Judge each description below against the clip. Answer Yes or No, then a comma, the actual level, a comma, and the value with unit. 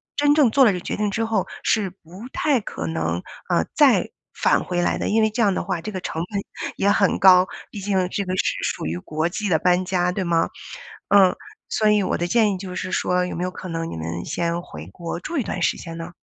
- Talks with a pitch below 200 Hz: Yes, medium, 185 Hz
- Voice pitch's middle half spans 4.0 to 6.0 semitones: No, average, 3.3 semitones